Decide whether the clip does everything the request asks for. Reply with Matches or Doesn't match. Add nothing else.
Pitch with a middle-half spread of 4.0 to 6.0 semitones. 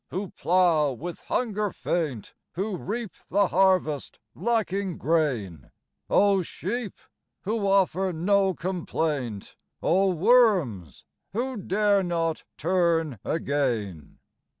Matches